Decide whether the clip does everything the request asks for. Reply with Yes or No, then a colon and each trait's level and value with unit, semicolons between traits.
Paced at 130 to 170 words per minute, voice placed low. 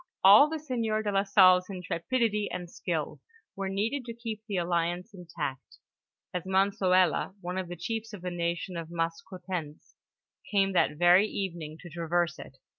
No: average, 155 wpm; medium, 185 Hz